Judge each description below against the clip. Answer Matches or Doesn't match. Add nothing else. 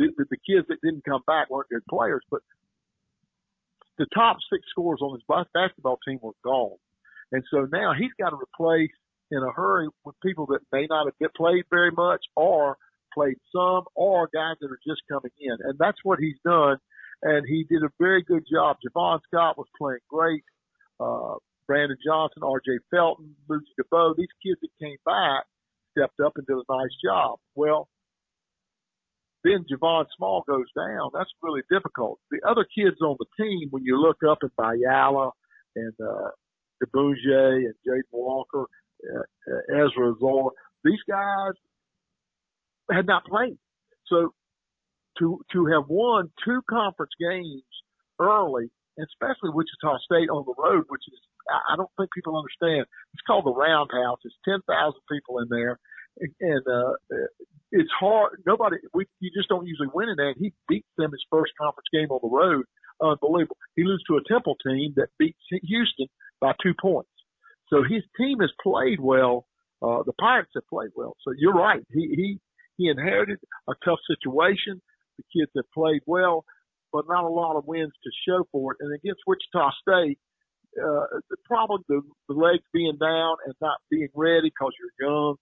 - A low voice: Doesn't match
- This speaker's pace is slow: Doesn't match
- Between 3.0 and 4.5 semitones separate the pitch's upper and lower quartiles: Doesn't match